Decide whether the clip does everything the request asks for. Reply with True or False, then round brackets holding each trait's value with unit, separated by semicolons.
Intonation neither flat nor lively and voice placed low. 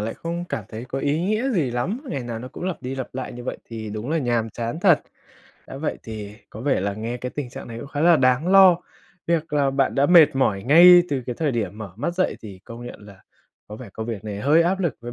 False (6.1 semitones; 130 Hz)